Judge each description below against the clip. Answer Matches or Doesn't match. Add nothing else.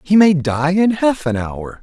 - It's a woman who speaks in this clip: Doesn't match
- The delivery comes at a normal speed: Doesn't match